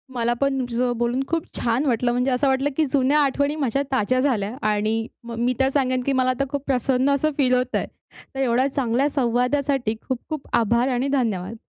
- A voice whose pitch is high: Yes, very high, 255 Hz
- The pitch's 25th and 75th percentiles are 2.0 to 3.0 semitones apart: Yes, narrow, 2.6 semitones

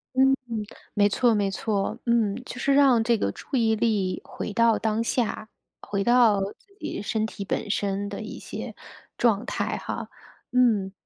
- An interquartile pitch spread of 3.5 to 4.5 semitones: No, average, 2.8 semitones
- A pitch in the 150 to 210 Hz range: No, high, 220 Hz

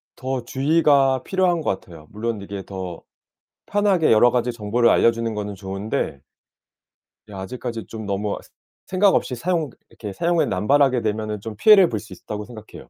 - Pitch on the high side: No, low, 115 Hz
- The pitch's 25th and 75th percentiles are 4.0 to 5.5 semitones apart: Yes, average, 5.2 semitones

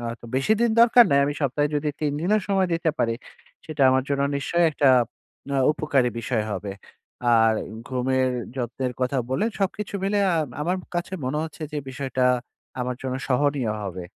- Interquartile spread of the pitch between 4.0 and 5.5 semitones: Yes, average, 4.3 semitones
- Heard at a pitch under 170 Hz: Yes, medium, 140 Hz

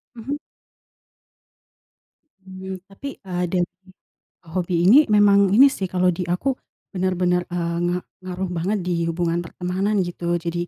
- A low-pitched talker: No, medium, 185 Hz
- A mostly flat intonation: Yes, narrow, 1.8 semitones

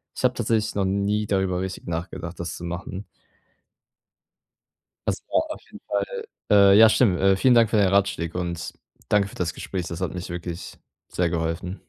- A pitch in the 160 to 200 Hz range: No, very low, 95 Hz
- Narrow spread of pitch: No, average, 3.2 semitones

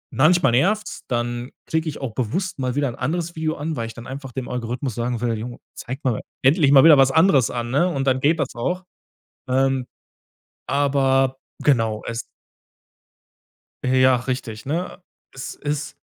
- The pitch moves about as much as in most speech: Yes, average, 3.5 semitones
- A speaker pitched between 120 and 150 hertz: Yes, low, 135 Hz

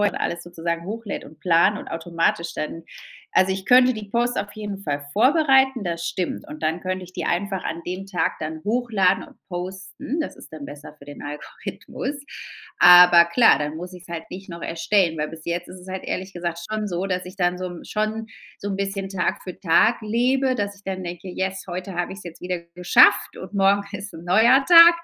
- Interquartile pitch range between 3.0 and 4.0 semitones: Yes, average, 3.3 semitones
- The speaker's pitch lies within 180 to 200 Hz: Yes, medium, 185 Hz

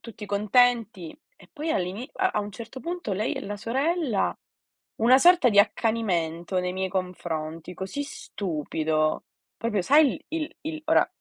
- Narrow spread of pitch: No, wide, 6.6 semitones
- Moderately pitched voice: No, high, 210 Hz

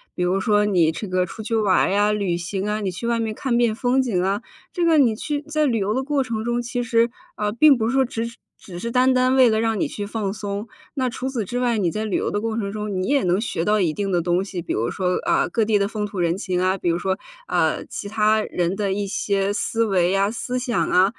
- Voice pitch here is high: Yes, high, 210 Hz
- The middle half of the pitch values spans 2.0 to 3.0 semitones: No, average, 3.6 semitones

